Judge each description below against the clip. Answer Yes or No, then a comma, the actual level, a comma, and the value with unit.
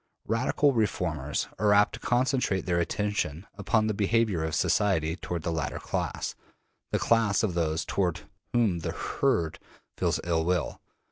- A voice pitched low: Yes, very low, 95 Hz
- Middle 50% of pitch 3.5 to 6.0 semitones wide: Yes, average, 4.6 semitones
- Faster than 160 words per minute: No, average, 150 wpm